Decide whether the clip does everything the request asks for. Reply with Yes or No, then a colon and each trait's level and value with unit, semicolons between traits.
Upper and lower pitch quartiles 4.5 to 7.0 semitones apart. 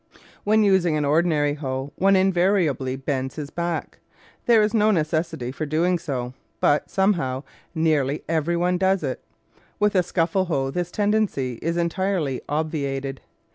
Yes: average, 5.0 semitones